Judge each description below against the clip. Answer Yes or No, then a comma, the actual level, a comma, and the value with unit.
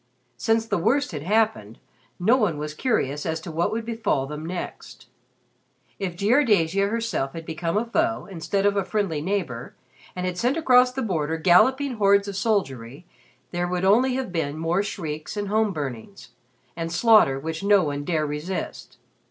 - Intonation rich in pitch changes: Yes, wide, 5.8 semitones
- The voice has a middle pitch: Yes, medium, 180 Hz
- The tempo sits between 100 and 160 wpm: No, average, 170 wpm